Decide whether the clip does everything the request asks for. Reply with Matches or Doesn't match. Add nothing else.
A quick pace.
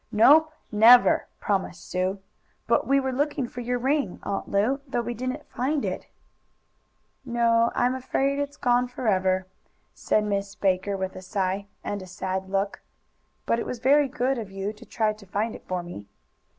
Doesn't match